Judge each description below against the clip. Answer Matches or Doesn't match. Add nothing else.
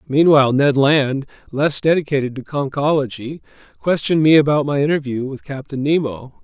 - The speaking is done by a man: Matches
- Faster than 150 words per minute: Doesn't match